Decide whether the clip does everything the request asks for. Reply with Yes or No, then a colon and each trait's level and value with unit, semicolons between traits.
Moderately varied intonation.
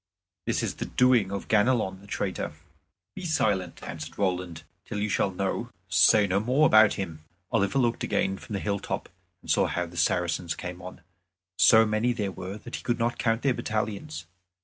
Yes: average, 3.7 semitones